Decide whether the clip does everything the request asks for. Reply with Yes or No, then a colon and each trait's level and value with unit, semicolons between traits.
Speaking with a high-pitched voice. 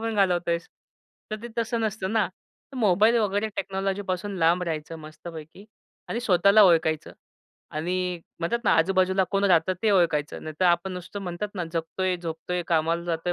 No: medium, 180 Hz